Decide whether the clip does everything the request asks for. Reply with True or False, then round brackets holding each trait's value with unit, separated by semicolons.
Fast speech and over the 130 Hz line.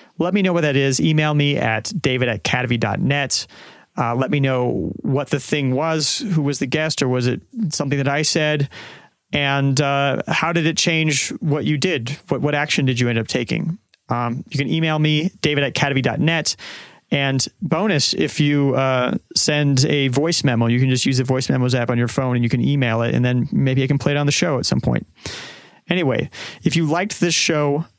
True (210 wpm; 140 Hz)